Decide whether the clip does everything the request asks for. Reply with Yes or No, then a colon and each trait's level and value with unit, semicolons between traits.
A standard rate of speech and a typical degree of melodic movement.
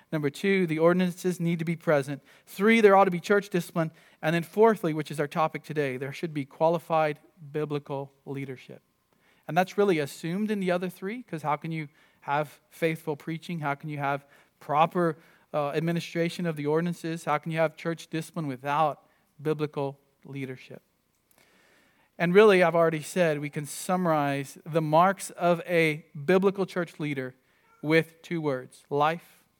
Yes: average, 165 wpm; average, 3.0 semitones